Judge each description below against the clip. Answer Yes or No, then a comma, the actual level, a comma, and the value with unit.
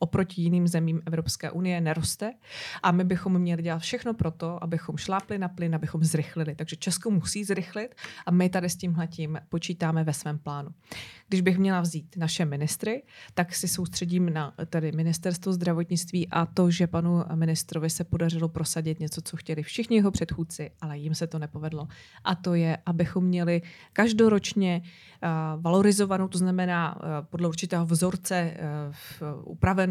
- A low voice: No, medium, 170 Hz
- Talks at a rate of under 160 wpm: No, average, 165 wpm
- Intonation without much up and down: Yes, narrow, 2.2 semitones